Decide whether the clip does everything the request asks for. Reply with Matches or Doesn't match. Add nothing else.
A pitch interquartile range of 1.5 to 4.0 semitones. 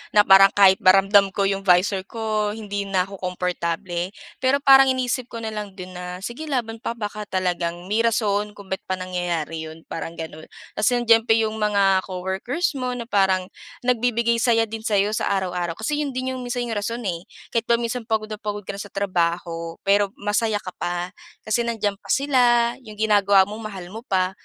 Matches